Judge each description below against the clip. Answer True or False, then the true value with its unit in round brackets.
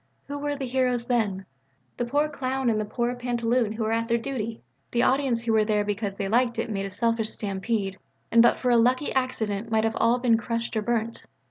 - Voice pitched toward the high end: True (230 Hz)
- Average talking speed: False (225 wpm)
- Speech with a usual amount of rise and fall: False (2.3 semitones)